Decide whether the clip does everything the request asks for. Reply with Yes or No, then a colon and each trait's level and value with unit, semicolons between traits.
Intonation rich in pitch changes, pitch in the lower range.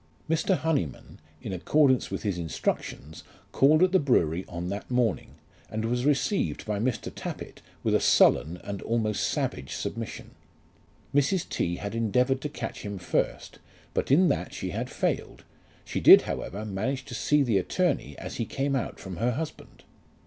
Yes: wide, 5.9 semitones; low, 115 Hz